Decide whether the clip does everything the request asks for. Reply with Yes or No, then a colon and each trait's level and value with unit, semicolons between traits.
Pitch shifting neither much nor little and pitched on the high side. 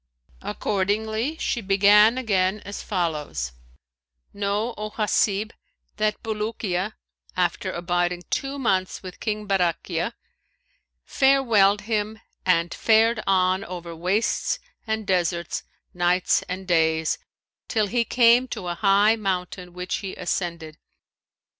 Yes: average, 3.5 semitones; high, 195 Hz